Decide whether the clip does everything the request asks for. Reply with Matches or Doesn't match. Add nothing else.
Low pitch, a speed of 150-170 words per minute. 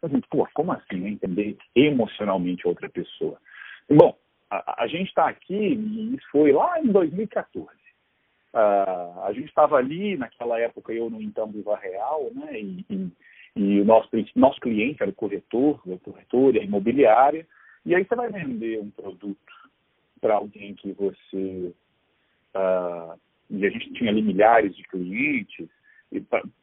Matches